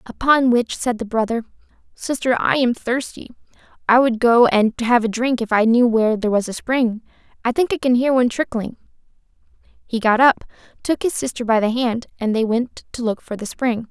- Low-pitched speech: No, high, 240 Hz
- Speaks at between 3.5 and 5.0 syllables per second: No, 5.4 syllables/s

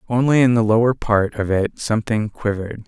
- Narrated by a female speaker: No, male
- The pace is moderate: Yes, average, 190 wpm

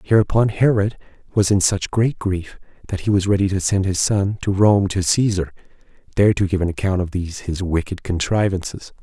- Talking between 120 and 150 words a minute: No, average, 195 wpm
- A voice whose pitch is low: Yes, very low, 95 Hz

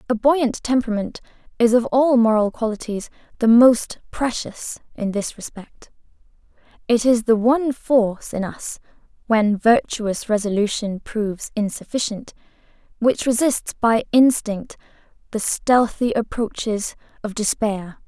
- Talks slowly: Yes, slow, 110 wpm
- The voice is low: No, high, 230 Hz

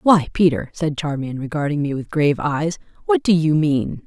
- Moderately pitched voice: Yes, medium, 155 Hz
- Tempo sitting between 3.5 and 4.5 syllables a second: No, 4.9 syllables/s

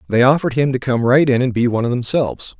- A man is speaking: Yes, male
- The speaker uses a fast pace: Yes, fast, 280 wpm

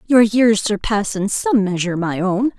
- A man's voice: No, female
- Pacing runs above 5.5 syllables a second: No, 4.5 syllables/s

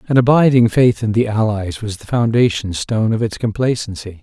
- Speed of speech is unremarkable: Yes, average, 185 wpm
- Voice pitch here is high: No, low, 110 Hz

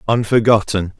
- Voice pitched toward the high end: No, low, 105 Hz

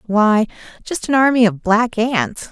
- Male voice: No, female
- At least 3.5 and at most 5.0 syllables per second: Yes, 4.0 syllables/s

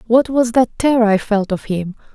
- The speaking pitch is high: Yes, high, 225 Hz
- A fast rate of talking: Yes, fast, 225 wpm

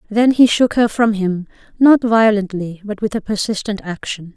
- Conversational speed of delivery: Yes, average, 180 wpm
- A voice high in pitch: Yes, high, 210 Hz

